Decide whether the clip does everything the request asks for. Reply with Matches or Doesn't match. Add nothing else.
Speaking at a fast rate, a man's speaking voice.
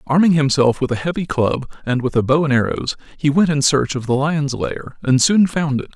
Matches